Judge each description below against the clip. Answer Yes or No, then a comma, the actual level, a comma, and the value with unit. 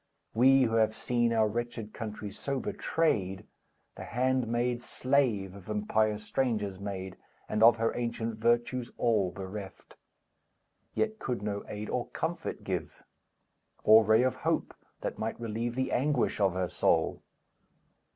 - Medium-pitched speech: No, low, 115 Hz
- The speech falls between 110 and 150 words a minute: Yes, average, 140 wpm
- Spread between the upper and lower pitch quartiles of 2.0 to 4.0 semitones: Yes, average, 2.9 semitones